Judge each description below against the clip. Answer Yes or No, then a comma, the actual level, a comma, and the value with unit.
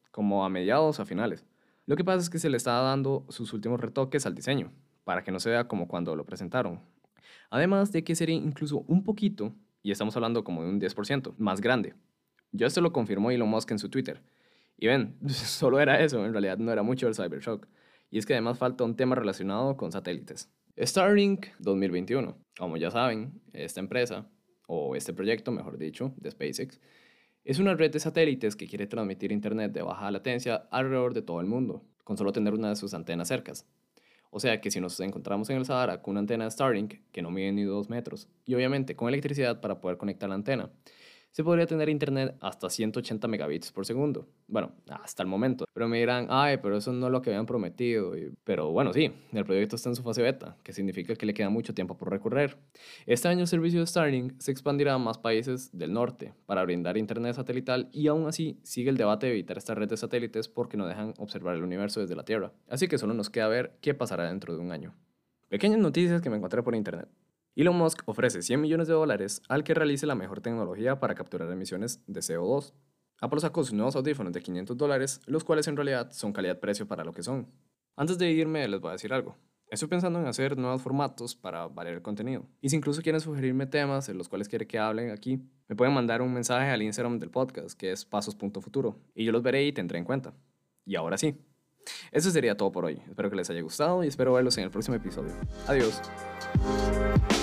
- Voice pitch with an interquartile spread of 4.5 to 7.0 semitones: Yes, wide, 5.5 semitones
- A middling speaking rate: No, fast, 220 wpm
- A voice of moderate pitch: No, low, 125 Hz